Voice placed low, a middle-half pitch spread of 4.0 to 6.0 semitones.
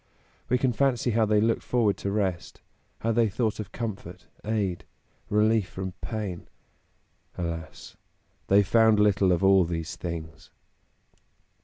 No: low, 105 Hz; average, 3.4 semitones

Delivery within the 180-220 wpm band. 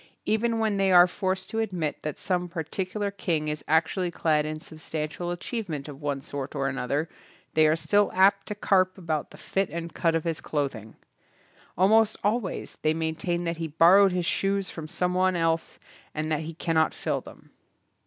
Yes: average, 185 wpm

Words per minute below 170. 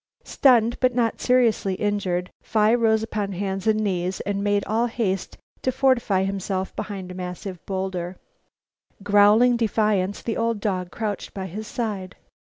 Yes: average, 150 wpm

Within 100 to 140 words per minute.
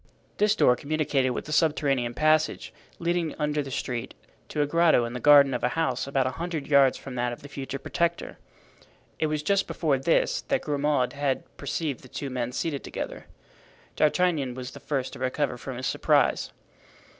No: average, 185 wpm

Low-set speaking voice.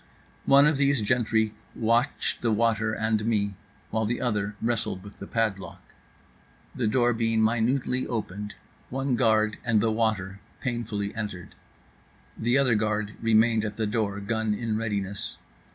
Yes: low, 110 Hz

